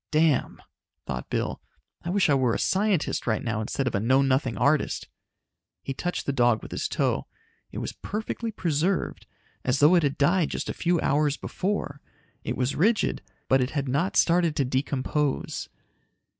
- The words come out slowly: No, average, 175 wpm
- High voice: No, medium, 145 Hz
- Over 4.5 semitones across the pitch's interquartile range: Yes, average, 4.9 semitones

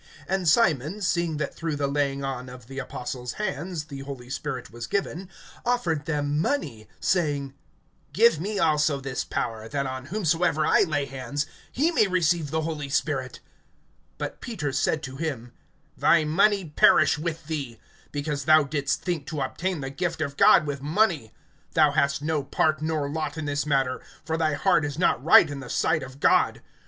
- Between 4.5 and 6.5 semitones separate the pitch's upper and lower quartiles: No, average, 3.1 semitones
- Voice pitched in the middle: Yes, medium, 150 Hz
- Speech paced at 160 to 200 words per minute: Yes, average, 180 wpm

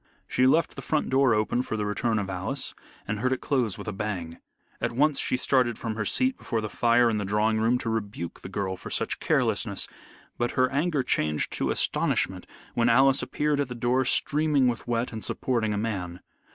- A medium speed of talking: No, fast, 210 wpm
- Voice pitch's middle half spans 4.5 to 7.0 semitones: No, average, 3.7 semitones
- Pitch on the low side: Yes, low, 115 Hz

